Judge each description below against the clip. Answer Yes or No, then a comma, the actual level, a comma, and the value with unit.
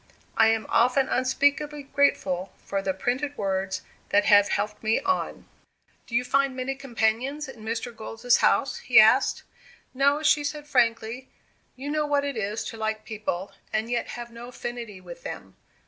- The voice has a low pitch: No, high, 240 Hz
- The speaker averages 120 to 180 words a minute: Yes, average, 165 wpm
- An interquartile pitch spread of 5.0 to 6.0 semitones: No, average, 4.2 semitones